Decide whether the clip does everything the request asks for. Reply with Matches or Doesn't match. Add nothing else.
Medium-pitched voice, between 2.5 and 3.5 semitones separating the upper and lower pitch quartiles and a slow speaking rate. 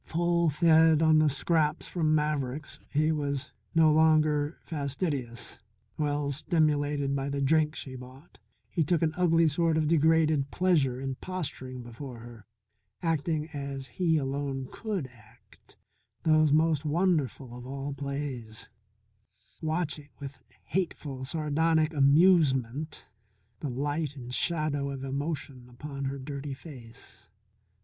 Matches